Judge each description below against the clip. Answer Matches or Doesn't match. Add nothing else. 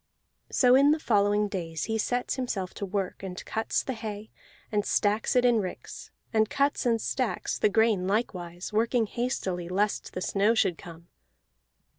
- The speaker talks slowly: Doesn't match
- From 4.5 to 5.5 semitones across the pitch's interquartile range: Doesn't match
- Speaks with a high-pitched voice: Matches